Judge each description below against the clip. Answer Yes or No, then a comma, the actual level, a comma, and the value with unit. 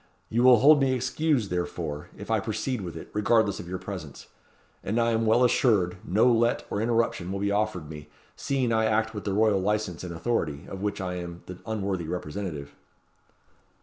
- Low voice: Yes, low, 105 Hz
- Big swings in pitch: No, average, 4.4 semitones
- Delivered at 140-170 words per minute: No, average, 190 wpm